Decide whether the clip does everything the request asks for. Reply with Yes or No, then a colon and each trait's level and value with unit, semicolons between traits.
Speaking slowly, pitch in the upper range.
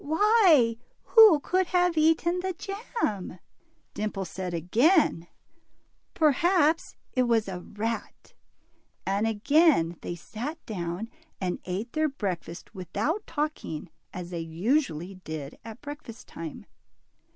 Yes: slow, 120 wpm; high, 230 Hz